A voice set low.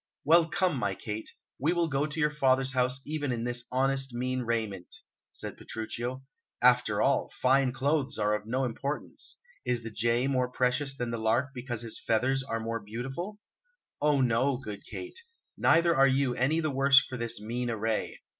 Yes: low, 130 Hz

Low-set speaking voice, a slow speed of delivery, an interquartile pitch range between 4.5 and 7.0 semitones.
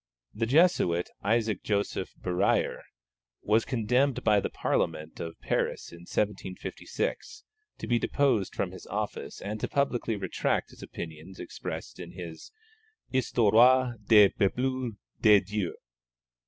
Yes: low, 105 Hz; slow, 125 wpm; average, 4.8 semitones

